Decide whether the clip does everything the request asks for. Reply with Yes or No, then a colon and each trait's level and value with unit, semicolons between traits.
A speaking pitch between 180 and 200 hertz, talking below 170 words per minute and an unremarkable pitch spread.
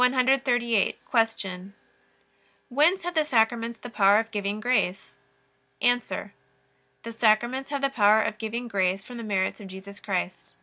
No: high, 225 Hz; average, 140 wpm; average, 3.6 semitones